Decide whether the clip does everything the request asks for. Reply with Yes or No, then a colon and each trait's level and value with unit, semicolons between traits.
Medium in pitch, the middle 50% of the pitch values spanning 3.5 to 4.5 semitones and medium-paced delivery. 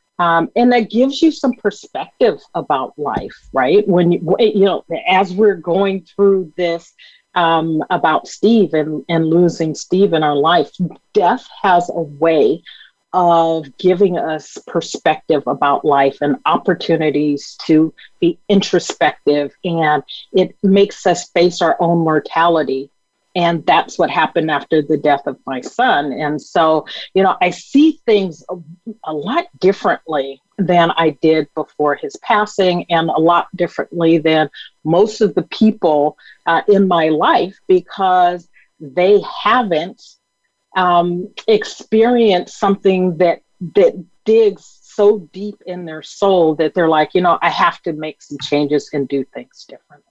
Yes: medium, 175 Hz; average, 3.9 semitones; average, 145 wpm